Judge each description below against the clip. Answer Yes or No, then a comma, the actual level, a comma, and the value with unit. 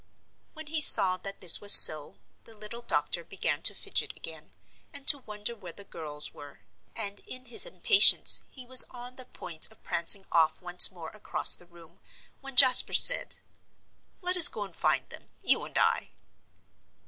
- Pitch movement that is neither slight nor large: No, wide, 6.5 semitones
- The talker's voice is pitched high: Yes, high, 210 Hz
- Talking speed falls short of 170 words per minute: No, average, 175 wpm